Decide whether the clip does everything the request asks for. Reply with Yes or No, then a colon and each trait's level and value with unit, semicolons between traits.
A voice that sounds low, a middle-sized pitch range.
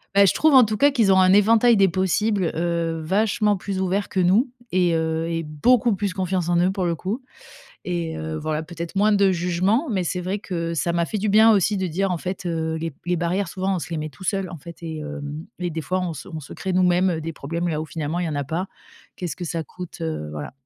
No: medium, 180 Hz; average, 3.1 semitones